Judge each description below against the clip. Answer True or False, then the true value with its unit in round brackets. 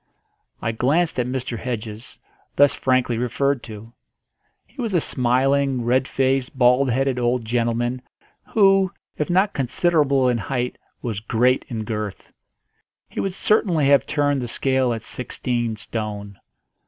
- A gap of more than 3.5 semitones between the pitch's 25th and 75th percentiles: False (2.9 semitones)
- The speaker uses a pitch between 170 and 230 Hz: False (125 Hz)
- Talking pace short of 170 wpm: True (140 wpm)